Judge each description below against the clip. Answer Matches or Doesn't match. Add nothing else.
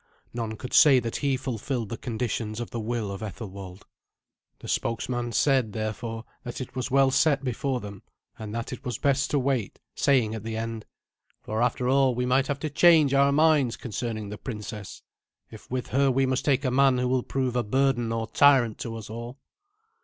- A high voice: Doesn't match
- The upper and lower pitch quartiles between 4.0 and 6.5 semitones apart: Doesn't match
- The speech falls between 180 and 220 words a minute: Matches